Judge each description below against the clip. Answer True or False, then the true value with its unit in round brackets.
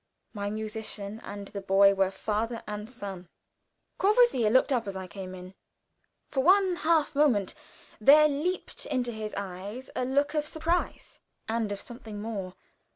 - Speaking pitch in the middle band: False (220 Hz)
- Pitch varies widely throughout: True (5.9 semitones)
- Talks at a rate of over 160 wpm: False (155 wpm)